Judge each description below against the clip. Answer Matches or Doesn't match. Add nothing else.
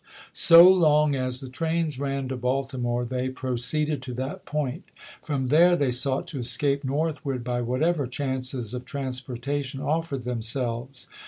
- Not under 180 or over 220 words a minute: Doesn't match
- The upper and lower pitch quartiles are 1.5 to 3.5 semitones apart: Matches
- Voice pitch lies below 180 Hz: Matches